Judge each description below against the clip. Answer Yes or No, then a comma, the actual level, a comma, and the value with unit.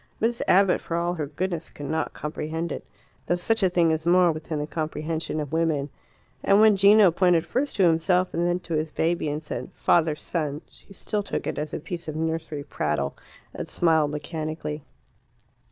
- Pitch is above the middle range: No, medium, 165 Hz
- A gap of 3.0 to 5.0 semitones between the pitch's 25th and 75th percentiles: No, narrow, 2.5 semitones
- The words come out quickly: No, average, 190 wpm